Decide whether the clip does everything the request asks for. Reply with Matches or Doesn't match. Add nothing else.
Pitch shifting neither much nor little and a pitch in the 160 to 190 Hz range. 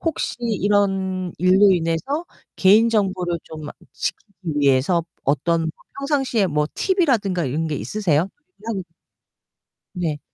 Matches